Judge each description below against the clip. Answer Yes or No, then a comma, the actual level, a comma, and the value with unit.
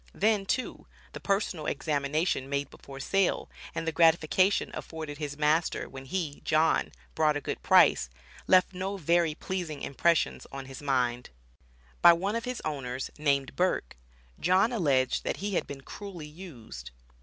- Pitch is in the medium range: Yes, medium, 155 Hz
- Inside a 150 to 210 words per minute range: Yes, average, 155 wpm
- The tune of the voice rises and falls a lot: No, average, 4.9 semitones